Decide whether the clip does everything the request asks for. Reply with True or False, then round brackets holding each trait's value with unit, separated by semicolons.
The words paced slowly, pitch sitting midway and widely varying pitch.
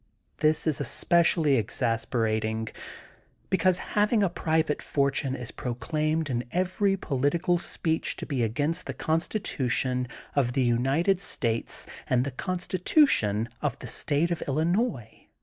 True (130 wpm; 150 Hz; 5.7 semitones)